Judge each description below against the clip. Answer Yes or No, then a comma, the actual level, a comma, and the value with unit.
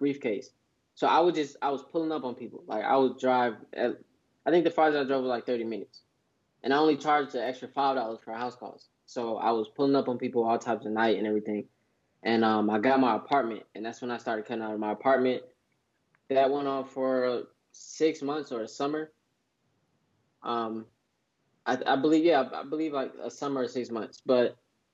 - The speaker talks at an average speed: No, fast, 215 wpm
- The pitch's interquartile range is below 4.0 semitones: Yes, average, 3.4 semitones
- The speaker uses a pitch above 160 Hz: No, low, 130 Hz